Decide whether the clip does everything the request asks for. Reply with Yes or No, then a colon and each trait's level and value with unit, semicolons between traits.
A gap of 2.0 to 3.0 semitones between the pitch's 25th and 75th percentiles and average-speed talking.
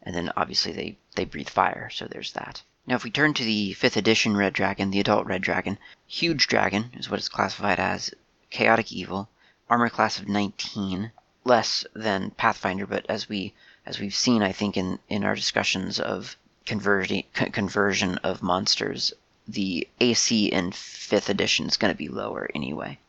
Yes: narrow, 2.4 semitones; average, 180 wpm